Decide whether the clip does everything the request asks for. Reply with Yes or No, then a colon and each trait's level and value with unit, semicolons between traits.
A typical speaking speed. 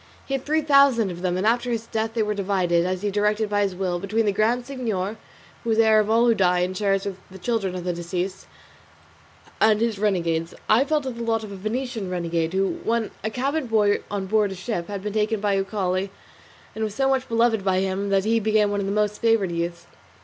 No: fast, 235 wpm